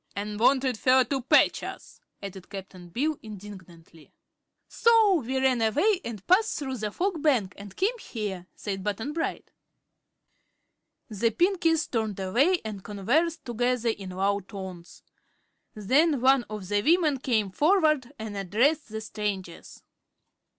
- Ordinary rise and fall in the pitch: No, wide, 6.5 semitones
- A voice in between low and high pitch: No, high, 230 Hz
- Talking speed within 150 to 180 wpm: No, slow, 135 wpm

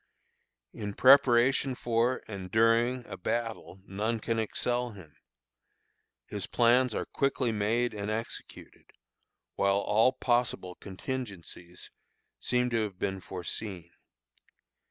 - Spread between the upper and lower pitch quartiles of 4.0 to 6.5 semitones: No, average, 3.6 semitones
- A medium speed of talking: No, slow, 110 wpm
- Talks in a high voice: No, low, 115 Hz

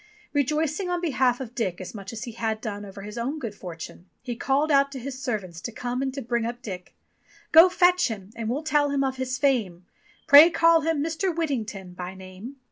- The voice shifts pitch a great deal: Yes, wide, 5.7 semitones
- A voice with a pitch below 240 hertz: No, very high, 250 Hz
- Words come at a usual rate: No, fast, 215 wpm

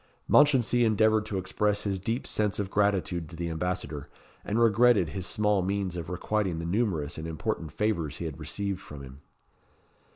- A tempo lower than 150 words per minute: No, average, 170 wpm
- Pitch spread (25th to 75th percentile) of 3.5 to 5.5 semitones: Yes, average, 4.2 semitones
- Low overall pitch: Yes, very low, 95 Hz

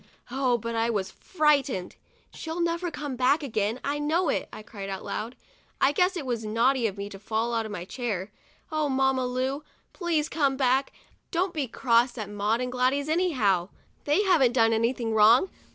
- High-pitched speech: Yes, very high, 255 Hz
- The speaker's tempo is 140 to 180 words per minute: No, average, 190 wpm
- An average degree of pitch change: Yes, average, 4.8 semitones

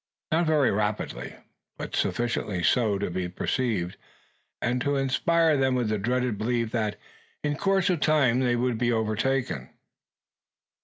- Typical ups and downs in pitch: Yes, average, 4.0 semitones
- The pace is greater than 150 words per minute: No, average, 145 wpm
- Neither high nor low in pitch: No, low, 120 Hz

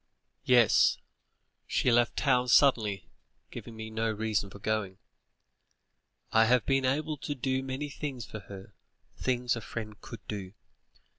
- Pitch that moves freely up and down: No, average, 3.4 semitones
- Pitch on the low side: Yes, low, 115 Hz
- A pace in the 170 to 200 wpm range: No, average, 140 wpm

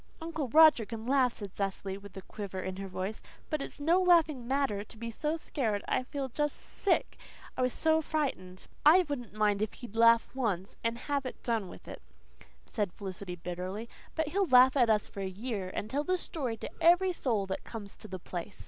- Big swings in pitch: Yes, wide, 6.4 semitones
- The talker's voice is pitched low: No, high, 230 Hz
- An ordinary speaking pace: No, fast, 210 wpm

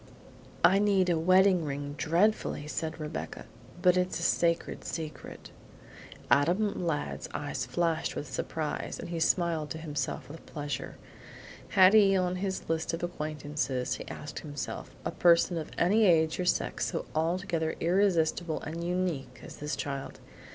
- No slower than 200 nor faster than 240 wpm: No, average, 150 wpm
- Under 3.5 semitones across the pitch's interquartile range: Yes, average, 3.1 semitones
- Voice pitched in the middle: Yes, medium, 165 Hz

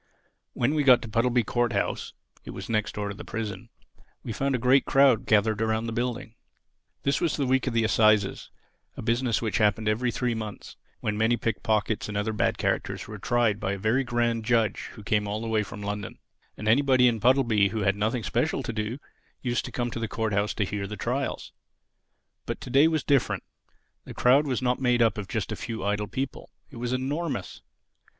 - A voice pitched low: Yes, low, 115 Hz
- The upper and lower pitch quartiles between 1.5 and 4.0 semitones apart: Yes, average, 2.8 semitones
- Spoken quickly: Yes, fast, 215 wpm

